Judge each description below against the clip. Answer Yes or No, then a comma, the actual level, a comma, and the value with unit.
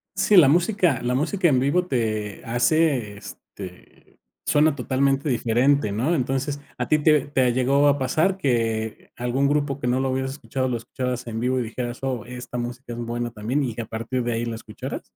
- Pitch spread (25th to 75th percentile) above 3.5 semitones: No, average, 3.1 semitones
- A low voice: Yes, low, 130 Hz